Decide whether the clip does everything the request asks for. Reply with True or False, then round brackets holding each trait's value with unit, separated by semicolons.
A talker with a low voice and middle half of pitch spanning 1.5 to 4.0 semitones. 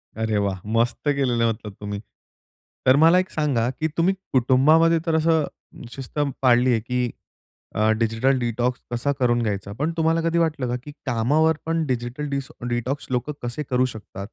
False (125 Hz; 4.4 semitones)